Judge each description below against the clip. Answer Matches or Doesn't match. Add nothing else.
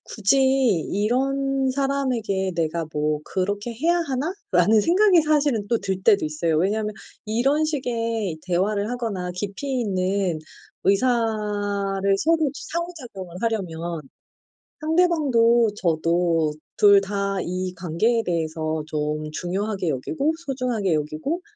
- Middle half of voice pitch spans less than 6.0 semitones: Doesn't match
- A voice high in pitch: Matches